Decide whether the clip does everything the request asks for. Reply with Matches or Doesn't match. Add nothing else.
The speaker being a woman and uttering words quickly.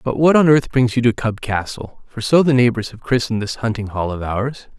Doesn't match